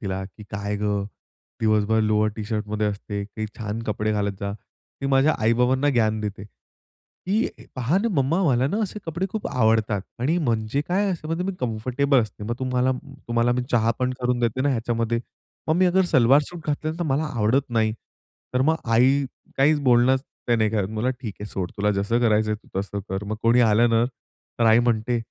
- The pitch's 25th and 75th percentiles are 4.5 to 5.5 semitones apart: No, average, 3.9 semitones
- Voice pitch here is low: Yes, low, 115 Hz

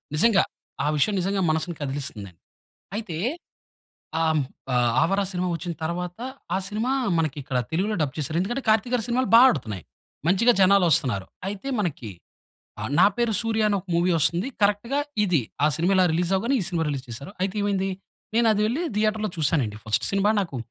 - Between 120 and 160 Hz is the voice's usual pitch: No, medium, 185 Hz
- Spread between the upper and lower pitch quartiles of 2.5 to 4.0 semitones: No, average, 5.3 semitones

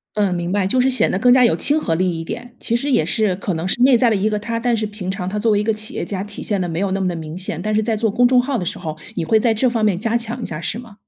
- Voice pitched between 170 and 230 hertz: Yes, high, 210 Hz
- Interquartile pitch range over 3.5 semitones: Yes, average, 4.0 semitones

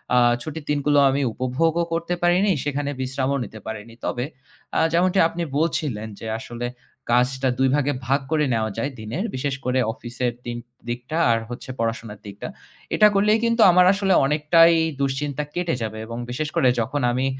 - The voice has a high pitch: No, medium, 140 Hz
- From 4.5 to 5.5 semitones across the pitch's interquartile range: Yes, average, 5.1 semitones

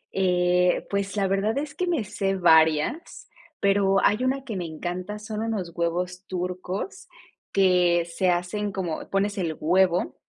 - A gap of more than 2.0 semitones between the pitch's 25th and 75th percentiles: Yes, narrow, 2.5 semitones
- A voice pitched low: No, high, 190 Hz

